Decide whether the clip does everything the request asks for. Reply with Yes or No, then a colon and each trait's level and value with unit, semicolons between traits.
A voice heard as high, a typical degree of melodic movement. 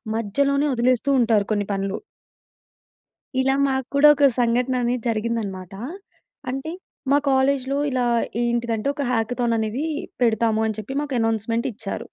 Yes: high, 240 Hz; average, 3.1 semitones